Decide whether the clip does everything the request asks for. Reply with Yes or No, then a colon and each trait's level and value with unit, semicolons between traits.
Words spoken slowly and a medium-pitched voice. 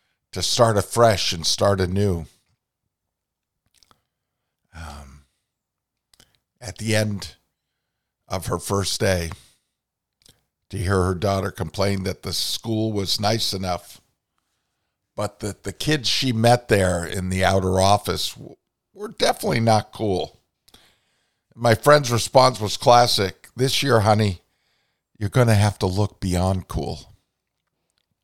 No: slow, 120 wpm; low, 100 Hz